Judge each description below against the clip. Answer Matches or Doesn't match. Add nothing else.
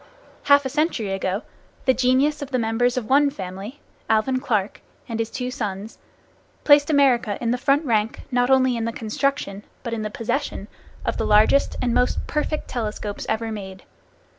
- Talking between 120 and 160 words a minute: Doesn't match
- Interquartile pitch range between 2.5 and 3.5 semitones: Doesn't match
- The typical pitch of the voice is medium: Doesn't match